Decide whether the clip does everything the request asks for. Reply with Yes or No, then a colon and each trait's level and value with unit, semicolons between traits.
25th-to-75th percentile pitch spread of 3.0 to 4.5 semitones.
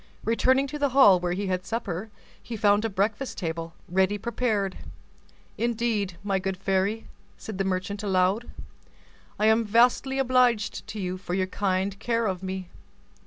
Yes: average, 3.6 semitones